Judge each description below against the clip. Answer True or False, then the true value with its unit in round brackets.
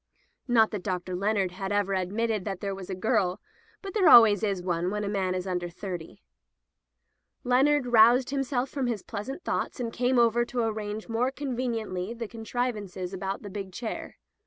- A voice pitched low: False (210 Hz)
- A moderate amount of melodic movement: True (4.1 semitones)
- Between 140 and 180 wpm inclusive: True (175 wpm)